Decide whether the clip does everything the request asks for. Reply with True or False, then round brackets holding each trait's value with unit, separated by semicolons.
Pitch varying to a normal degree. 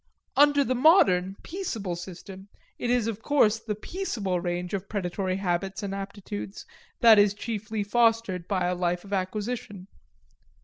True (3.6 semitones)